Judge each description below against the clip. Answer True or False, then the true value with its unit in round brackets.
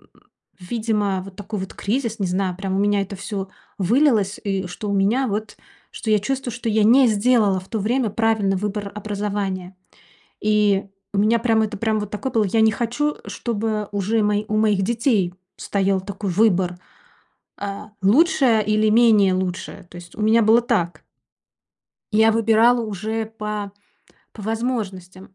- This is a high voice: True (210 Hz)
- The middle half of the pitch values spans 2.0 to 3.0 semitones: True (2.4 semitones)